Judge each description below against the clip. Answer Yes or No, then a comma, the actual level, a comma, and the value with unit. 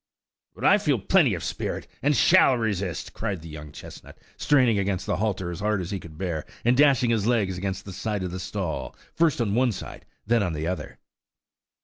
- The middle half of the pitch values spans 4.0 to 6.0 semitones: Yes, average, 4.3 semitones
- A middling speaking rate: No, fast, 210 wpm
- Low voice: Yes, low, 100 Hz